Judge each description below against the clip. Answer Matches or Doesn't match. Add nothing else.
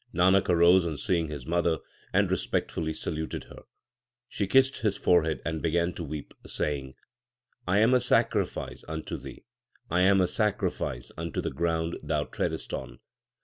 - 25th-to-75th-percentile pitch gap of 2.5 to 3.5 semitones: Matches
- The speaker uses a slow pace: Doesn't match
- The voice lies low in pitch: Matches